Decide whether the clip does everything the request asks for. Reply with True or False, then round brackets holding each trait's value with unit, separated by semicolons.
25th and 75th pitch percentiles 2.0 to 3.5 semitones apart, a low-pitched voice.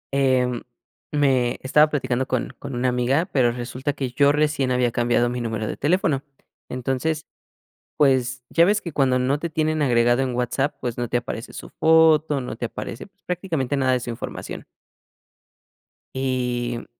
True (3.2 semitones; 130 Hz)